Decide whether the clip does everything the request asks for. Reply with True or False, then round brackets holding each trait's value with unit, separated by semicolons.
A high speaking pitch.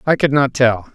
False (130 Hz)